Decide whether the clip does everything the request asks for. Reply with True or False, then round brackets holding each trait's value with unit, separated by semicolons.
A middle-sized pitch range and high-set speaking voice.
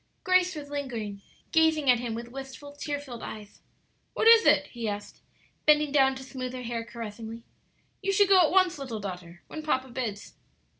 True (4.8 semitones; 265 Hz)